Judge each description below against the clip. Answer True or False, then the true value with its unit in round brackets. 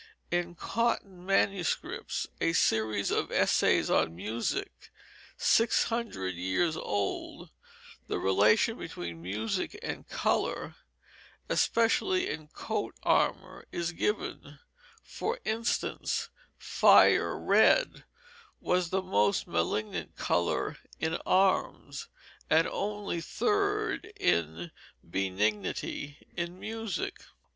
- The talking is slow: True (95 wpm)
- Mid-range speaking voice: True (170 Hz)